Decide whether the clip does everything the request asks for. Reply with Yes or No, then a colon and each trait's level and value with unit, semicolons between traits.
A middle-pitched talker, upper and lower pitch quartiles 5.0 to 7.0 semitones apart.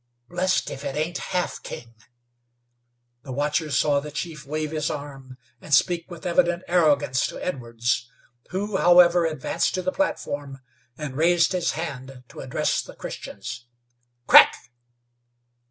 No: medium, 155 Hz; average, 4.2 semitones